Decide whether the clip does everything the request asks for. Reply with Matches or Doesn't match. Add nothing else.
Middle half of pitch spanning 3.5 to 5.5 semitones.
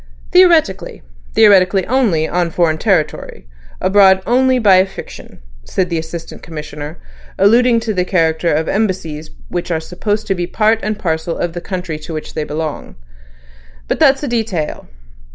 Matches